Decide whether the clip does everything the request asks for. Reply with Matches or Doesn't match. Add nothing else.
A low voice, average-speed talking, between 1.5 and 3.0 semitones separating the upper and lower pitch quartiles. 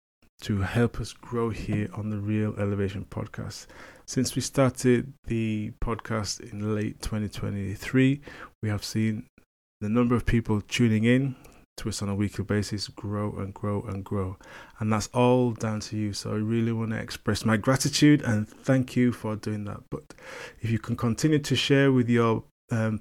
Matches